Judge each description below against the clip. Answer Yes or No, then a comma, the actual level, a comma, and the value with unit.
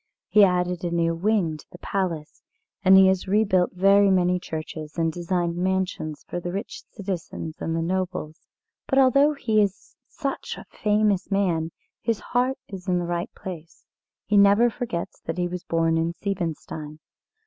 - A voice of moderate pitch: Yes, medium, 180 Hz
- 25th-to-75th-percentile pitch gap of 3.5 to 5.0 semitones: No, average, 3.1 semitones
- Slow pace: No, average, 170 wpm